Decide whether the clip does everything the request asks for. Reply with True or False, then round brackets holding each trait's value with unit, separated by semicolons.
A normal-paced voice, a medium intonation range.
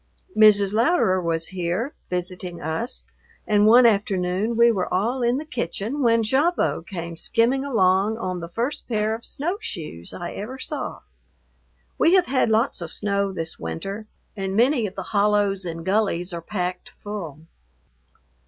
True (155 wpm; 4.6 semitones)